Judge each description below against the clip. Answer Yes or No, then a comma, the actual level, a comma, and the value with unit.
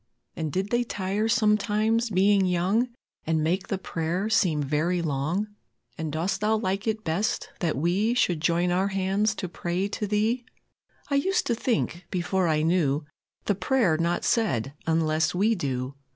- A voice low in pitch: No, medium, 185 Hz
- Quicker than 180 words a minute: No, average, 165 wpm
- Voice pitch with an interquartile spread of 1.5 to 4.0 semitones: No, average, 4.5 semitones